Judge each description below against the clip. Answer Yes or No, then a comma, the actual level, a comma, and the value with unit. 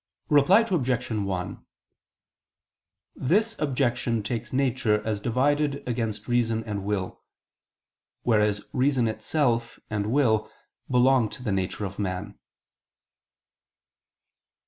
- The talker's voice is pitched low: Yes, low, 120 Hz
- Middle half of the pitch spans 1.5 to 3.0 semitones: No, average, 4.0 semitones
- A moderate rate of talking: No, slow, 100 wpm